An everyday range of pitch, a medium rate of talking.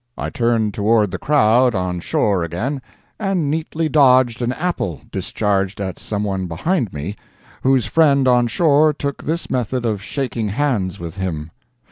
No: wide, 6.3 semitones; average, 150 wpm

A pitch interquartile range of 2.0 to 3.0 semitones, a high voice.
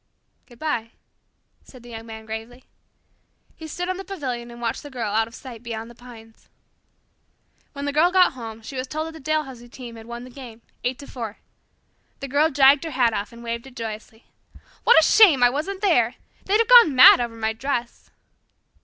No: average, 4.2 semitones; high, 245 Hz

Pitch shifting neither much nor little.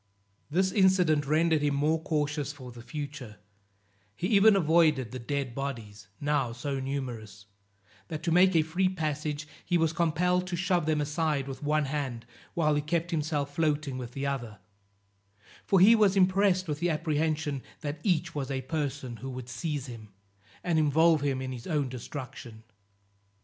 Yes: average, 3.6 semitones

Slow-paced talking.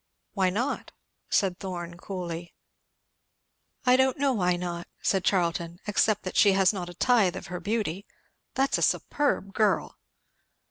No: average, 145 wpm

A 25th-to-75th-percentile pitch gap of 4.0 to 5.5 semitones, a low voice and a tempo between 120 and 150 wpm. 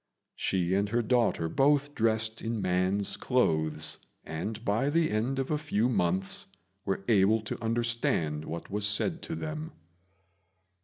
Yes: average, 4.8 semitones; low, 110 Hz; average, 145 wpm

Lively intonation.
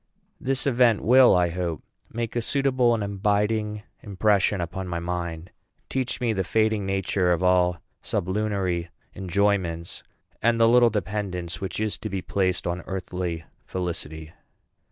No: average, 3.5 semitones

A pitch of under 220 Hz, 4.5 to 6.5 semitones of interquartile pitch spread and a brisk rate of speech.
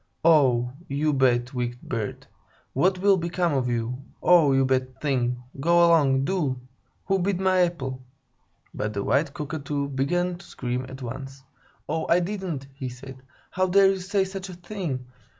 No: medium, 140 Hz; wide, 5.5 semitones; average, 165 wpm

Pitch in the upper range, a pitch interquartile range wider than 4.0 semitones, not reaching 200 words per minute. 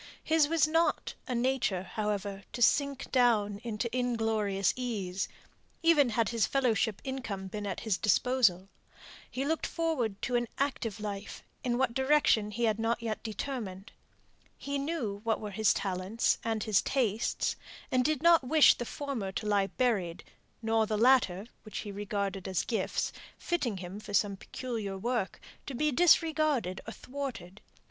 Yes: high, 225 Hz; average, 4.5 semitones; average, 155 wpm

